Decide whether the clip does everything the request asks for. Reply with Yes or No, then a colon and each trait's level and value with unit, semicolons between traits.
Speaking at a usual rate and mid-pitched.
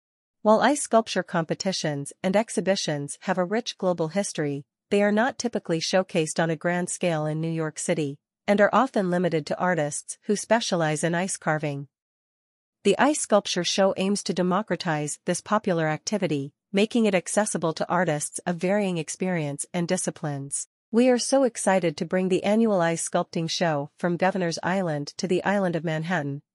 Yes: average, 165 wpm; medium, 180 Hz